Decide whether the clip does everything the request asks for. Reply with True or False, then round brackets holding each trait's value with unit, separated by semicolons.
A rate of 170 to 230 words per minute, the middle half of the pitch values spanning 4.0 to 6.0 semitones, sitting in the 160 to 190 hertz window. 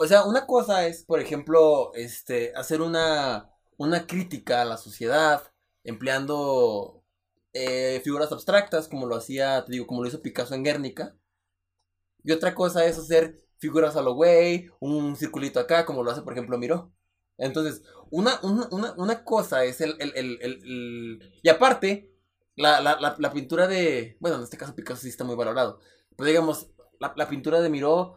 False (175 wpm; 5.0 semitones; 150 Hz)